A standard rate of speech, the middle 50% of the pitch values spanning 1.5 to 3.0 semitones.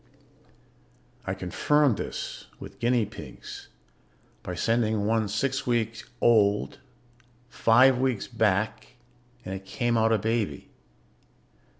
No: slow, 105 wpm; narrow, 2.5 semitones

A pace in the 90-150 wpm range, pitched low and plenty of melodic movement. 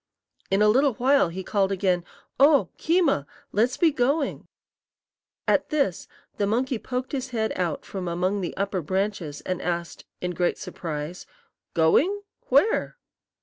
No: average, 145 wpm; high, 200 Hz; wide, 6.7 semitones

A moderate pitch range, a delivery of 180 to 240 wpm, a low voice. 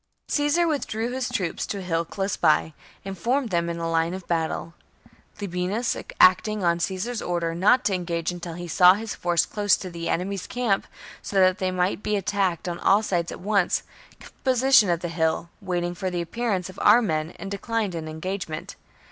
No: average, 3.4 semitones; average, 190 wpm; medium, 185 Hz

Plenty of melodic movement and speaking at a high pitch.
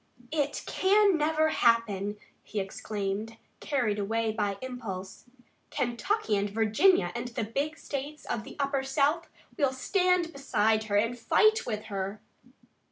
Yes: wide, 6.1 semitones; high, 235 Hz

